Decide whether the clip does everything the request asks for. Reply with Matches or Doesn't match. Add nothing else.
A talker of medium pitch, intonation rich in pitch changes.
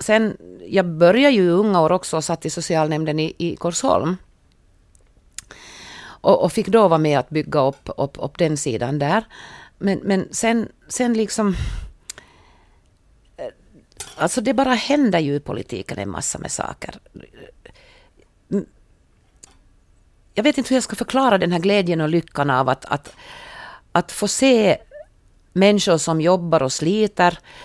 Matches